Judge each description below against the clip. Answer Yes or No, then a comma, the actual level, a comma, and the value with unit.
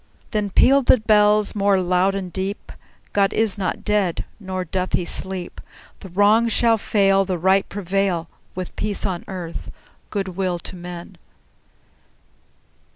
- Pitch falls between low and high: No, high, 195 Hz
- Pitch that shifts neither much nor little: No, narrow, 2.2 semitones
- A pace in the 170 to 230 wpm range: No, average, 145 wpm